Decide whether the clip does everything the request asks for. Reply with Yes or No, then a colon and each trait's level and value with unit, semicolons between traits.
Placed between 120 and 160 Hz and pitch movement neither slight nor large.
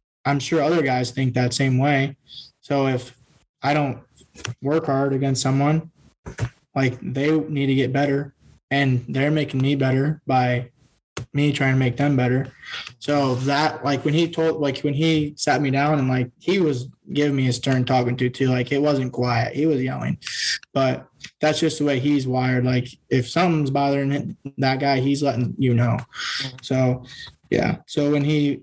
No: medium, 140 Hz; narrow, 2.3 semitones